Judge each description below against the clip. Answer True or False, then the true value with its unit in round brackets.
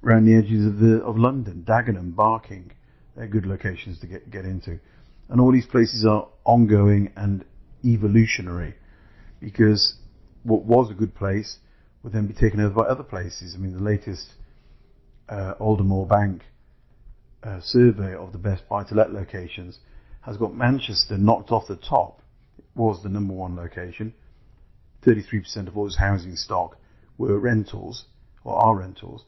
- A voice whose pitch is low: True (105 Hz)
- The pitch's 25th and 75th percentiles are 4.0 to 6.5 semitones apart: False (2.8 semitones)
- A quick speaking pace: False (155 wpm)